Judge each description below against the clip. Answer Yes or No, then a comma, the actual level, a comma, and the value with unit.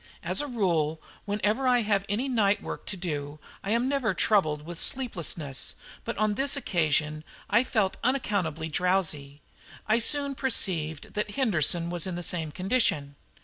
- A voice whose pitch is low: No, high, 195 Hz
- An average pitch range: No, wide, 6.5 semitones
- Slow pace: No, average, 155 wpm